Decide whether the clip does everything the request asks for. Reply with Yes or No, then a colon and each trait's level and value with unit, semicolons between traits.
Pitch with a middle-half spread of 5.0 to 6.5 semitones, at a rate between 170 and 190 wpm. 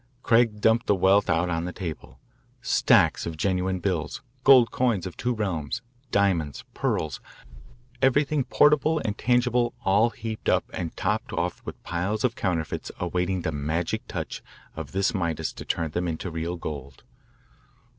No: wide, 5.6 semitones; average, 155 wpm